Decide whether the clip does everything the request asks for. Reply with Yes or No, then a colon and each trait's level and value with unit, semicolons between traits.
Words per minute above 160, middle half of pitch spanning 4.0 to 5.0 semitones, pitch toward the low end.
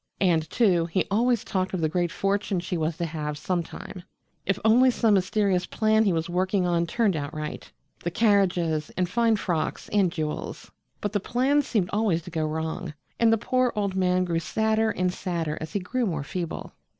No: average, 195 wpm; average, 4.3 semitones; medium, 185 Hz